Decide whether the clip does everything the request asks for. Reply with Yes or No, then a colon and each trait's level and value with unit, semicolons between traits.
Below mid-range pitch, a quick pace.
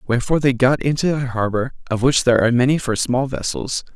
Yes: low, 130 Hz; fast, 215 wpm